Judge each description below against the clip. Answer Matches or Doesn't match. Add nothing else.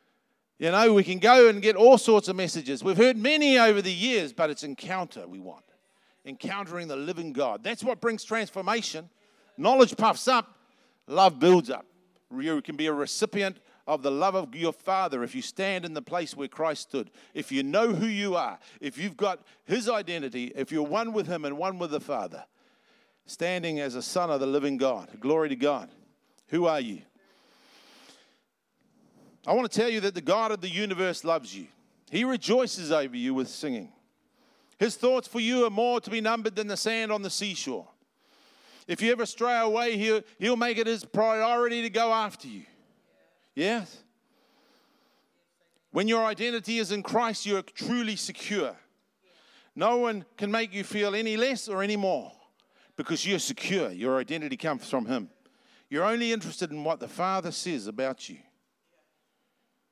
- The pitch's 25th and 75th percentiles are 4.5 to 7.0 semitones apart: Matches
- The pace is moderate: Matches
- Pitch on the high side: Matches